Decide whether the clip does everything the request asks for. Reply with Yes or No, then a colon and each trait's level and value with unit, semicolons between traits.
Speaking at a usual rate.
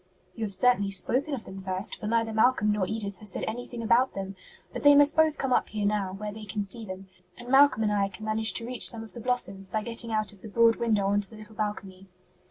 No: fast, 260 wpm